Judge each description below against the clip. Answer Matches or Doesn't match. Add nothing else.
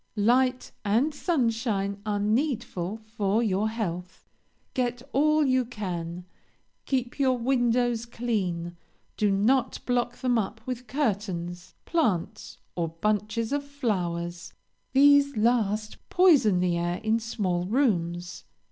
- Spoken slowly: Matches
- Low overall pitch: Doesn't match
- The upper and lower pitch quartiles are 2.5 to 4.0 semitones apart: Doesn't match